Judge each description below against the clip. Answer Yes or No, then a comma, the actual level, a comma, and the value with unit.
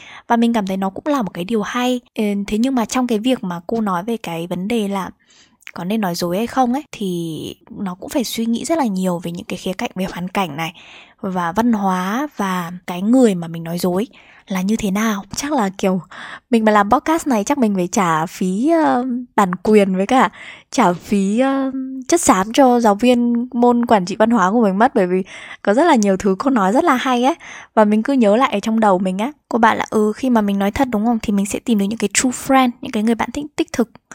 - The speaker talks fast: Yes, fast, 260 wpm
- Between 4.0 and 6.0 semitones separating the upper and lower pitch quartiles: Yes, average, 4.6 semitones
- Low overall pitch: No, high, 220 Hz